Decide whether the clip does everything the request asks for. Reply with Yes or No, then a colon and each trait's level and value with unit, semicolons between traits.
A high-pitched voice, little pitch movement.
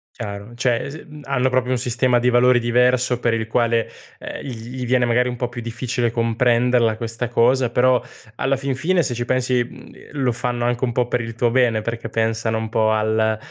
No: low, 120 Hz; narrow, 1.6 semitones